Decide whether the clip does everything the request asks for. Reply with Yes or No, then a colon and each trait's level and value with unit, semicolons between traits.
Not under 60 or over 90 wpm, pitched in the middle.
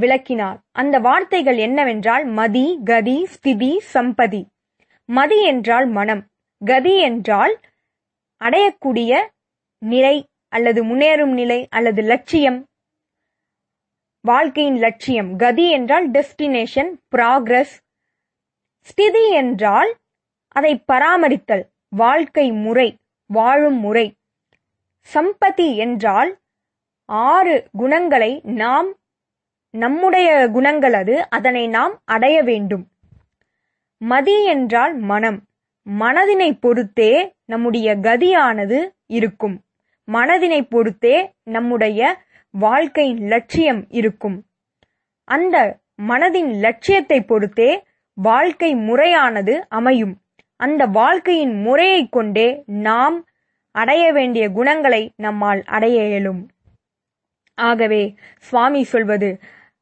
No: average, 80 wpm; very high, 250 Hz